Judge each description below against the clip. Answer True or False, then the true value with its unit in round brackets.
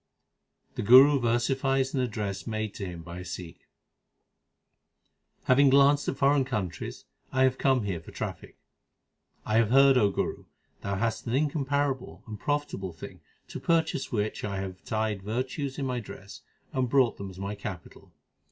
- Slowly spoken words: False (170 wpm)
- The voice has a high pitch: False (120 Hz)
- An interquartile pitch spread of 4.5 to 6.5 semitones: True (5.3 semitones)